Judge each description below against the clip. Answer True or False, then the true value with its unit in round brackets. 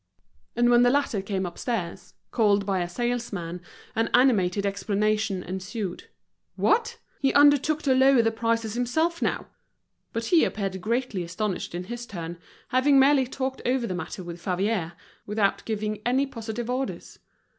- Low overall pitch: False (225 Hz)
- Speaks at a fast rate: False (150 wpm)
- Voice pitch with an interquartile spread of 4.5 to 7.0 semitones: True (4.9 semitones)